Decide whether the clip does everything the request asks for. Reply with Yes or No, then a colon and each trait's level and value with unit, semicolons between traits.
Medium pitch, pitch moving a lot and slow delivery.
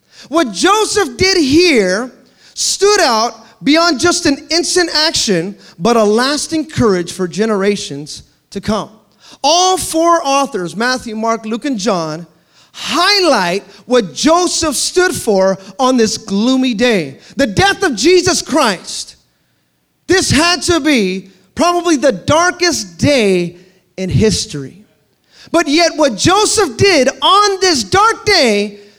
No: very high, 260 Hz; wide, 8.8 semitones; slow, 125 wpm